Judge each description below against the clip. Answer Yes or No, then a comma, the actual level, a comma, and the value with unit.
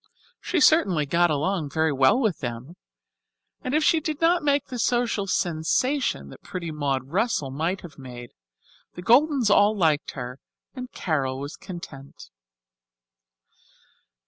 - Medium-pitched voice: Yes, medium, 175 Hz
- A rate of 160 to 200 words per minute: No, average, 140 wpm